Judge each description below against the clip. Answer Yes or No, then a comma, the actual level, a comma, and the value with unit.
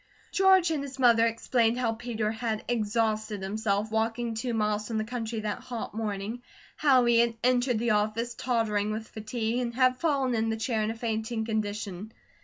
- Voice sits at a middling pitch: No, high, 225 Hz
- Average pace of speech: Yes, average, 185 wpm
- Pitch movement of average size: No, narrow, 1.9 semitones